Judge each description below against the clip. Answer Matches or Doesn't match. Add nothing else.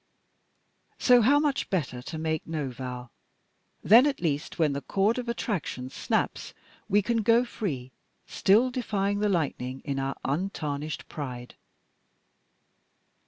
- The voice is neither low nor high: Matches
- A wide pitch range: Matches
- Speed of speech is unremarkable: Doesn't match